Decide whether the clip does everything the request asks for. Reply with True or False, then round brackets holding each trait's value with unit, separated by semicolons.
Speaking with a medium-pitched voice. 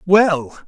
True (175 Hz)